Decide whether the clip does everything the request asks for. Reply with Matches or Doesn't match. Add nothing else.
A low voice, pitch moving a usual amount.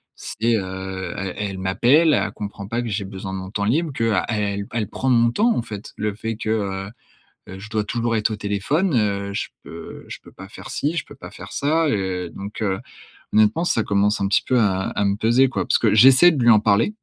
Matches